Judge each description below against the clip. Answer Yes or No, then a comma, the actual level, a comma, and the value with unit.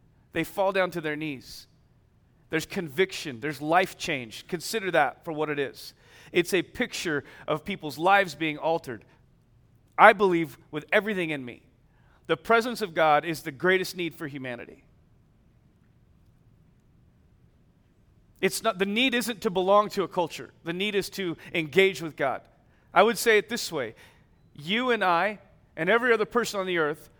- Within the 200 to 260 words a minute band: No, average, 165 wpm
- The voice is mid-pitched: Yes, medium, 165 Hz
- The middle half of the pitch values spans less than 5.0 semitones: No, average, 5.3 semitones